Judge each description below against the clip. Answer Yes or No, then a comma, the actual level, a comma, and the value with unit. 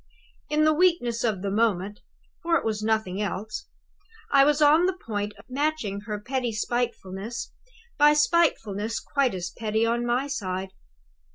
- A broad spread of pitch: Yes, wide, 5.9 semitones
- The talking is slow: No, average, 155 wpm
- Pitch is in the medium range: No, high, 230 Hz